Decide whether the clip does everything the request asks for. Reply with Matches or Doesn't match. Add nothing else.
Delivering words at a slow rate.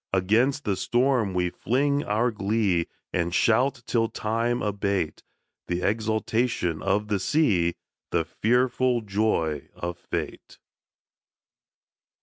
Matches